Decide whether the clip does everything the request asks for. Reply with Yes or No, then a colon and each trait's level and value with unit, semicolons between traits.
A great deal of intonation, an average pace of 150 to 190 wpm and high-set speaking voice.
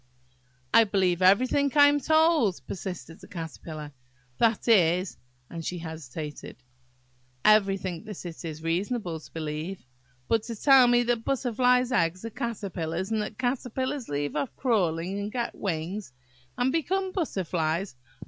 No: wide, 6.9 semitones; slow, 135 wpm; high, 195 Hz